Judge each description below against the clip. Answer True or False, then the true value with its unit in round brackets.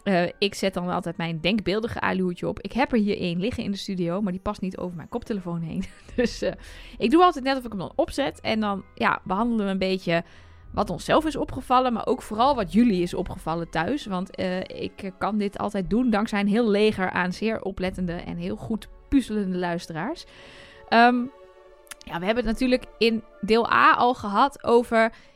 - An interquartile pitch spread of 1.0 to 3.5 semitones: False (4.3 semitones)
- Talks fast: True (205 wpm)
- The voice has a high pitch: True (205 Hz)